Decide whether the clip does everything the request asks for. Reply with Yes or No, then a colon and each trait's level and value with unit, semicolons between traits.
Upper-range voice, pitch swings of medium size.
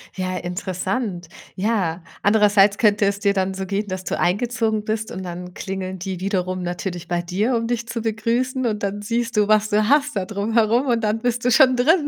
Yes: high, 210 Hz; average, 3.5 semitones